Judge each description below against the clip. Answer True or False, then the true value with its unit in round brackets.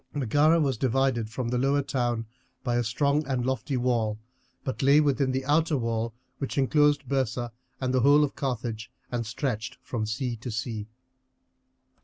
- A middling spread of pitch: True (3.1 semitones)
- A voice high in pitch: False (130 Hz)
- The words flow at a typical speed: True (165 wpm)